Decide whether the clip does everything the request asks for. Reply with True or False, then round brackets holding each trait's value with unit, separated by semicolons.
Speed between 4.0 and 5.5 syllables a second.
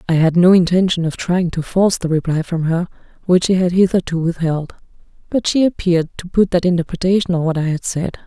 False (6.0 syllables/s)